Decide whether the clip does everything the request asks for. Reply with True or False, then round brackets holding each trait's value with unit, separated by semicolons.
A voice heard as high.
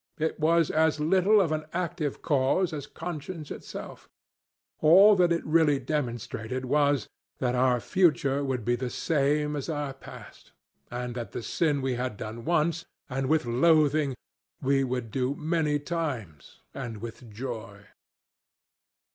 False (145 Hz)